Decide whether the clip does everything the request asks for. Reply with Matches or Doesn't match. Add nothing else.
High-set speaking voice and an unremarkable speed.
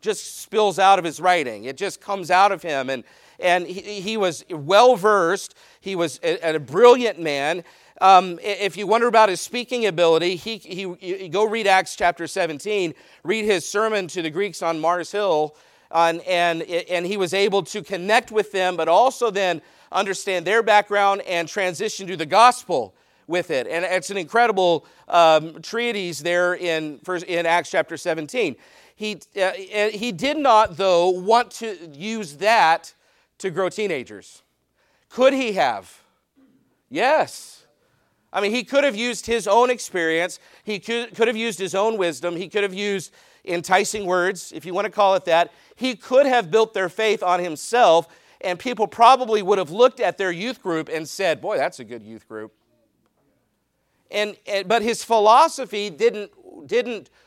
Matches